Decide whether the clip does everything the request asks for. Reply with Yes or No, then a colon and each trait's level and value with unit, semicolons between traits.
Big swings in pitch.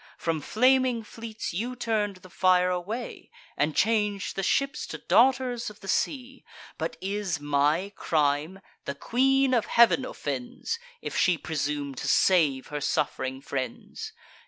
Yes: wide, 8.1 semitones